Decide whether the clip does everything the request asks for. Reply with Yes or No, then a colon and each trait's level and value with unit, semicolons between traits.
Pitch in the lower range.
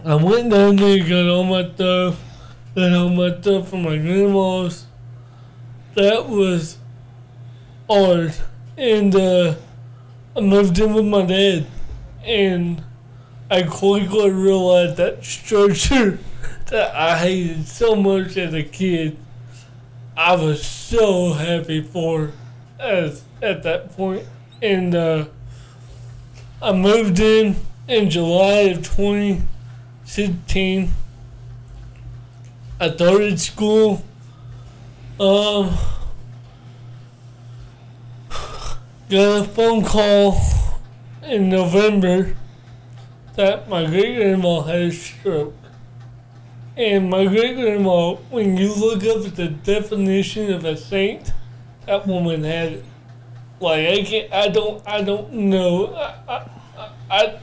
No: medium, 170 Hz